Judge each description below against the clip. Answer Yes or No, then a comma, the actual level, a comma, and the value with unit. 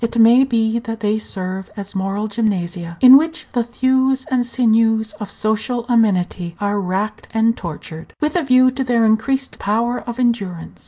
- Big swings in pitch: No, average, 3.5 semitones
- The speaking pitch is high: Yes, high, 225 Hz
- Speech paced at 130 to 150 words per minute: No, average, 170 wpm